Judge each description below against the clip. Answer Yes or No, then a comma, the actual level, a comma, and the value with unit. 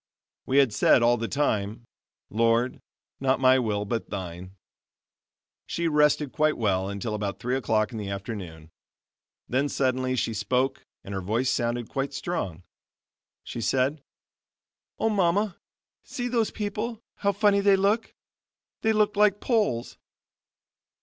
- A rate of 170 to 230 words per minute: No, slow, 135 wpm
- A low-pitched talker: Yes, low, 130 Hz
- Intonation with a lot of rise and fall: Yes, wide, 8.3 semitones